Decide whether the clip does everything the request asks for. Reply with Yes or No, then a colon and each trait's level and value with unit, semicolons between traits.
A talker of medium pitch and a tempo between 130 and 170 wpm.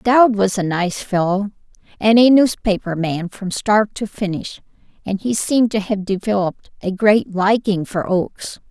No: high, 205 Hz; average, 165 wpm